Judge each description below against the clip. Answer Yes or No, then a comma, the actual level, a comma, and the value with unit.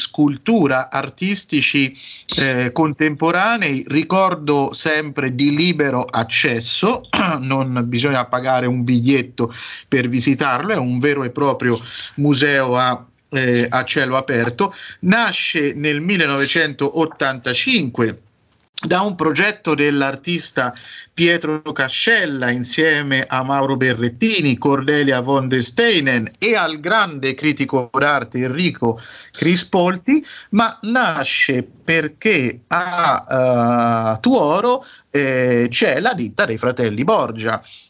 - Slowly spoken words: Yes, slow, 100 wpm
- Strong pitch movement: No, average, 4.3 semitones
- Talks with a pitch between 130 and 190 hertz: Yes, medium, 140 Hz